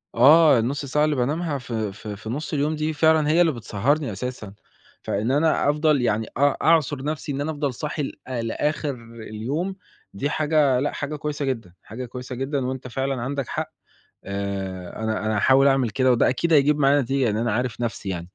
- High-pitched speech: No, low, 135 Hz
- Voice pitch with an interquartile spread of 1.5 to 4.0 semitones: No, average, 4.5 semitones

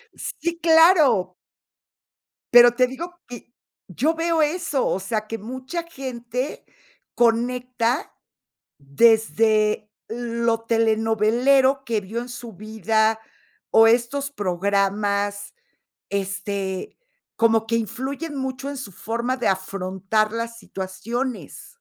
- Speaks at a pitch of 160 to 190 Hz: No, high, 230 Hz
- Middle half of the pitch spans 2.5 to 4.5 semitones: Yes, average, 3.6 semitones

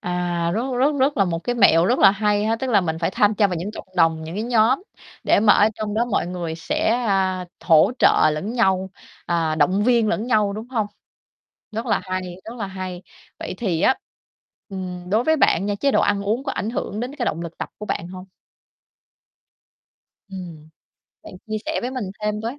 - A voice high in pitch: Yes, high, 205 Hz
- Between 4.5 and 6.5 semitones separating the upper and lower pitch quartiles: No, average, 4.1 semitones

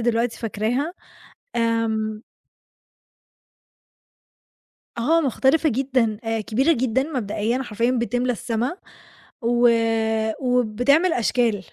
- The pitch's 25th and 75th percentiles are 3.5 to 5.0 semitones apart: No, average, 2.7 semitones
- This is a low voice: No, high, 240 Hz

